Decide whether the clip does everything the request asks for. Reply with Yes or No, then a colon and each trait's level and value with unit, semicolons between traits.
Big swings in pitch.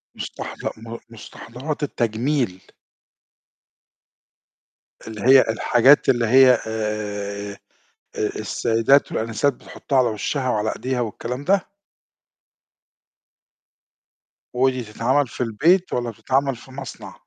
No: average, 3.3 semitones